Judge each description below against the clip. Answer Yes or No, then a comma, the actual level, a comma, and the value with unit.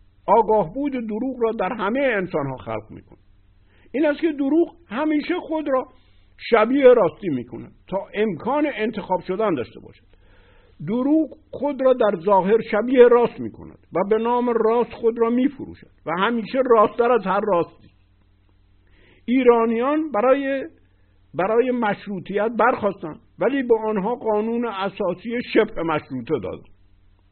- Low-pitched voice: No, high, 215 Hz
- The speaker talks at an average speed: Yes, average, 135 wpm